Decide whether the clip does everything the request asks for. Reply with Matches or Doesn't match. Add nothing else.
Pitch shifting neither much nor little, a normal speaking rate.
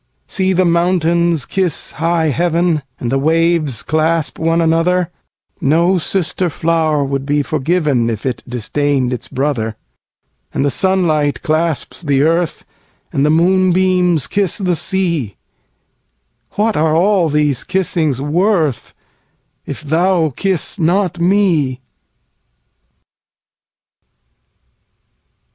Doesn't match